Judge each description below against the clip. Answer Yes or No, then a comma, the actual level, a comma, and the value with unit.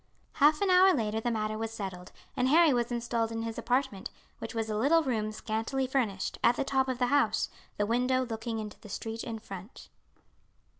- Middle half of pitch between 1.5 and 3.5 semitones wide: Yes, average, 3.2 semitones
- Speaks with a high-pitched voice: Yes, high, 230 Hz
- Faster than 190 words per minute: Yes, average, 200 wpm